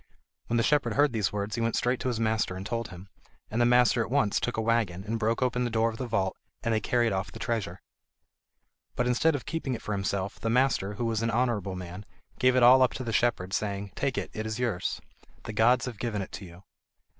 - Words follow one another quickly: Yes, fast, 250 wpm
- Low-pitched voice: Yes, low, 115 Hz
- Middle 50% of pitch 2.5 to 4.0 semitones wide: Yes, average, 3.3 semitones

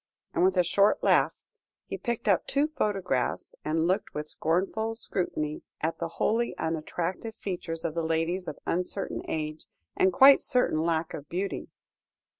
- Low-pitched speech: No, medium, 175 Hz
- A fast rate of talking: No, average, 155 wpm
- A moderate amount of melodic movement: Yes, average, 3.7 semitones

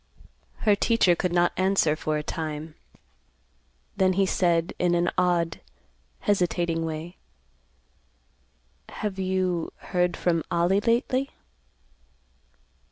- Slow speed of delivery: Yes, slow, 100 wpm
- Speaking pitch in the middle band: Yes, medium, 175 Hz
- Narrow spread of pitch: Yes, narrow, 2.3 semitones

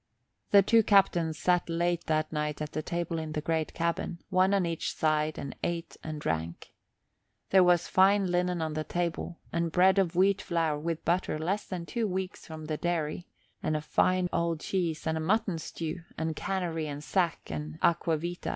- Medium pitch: Yes, medium, 170 Hz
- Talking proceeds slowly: No, average, 190 wpm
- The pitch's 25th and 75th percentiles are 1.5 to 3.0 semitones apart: Yes, narrow, 2.6 semitones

